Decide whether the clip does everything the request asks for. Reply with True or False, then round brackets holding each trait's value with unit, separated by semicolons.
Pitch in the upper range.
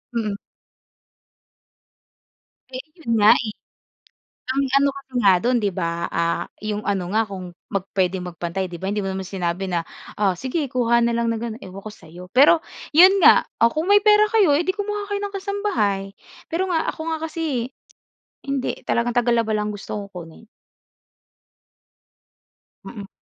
True (230 Hz)